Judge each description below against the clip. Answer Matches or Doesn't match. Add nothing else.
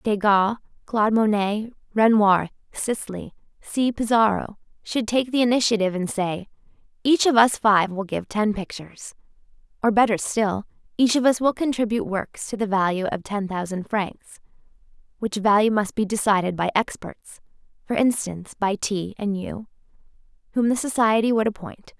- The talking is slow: Doesn't match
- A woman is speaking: Matches